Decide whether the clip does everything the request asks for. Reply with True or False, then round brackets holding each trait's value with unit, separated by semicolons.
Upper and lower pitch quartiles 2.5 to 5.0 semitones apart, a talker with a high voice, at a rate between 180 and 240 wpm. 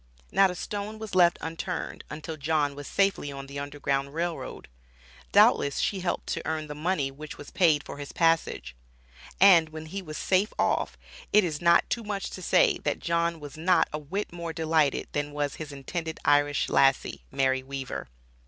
False (3.3 semitones; 155 Hz; 185 wpm)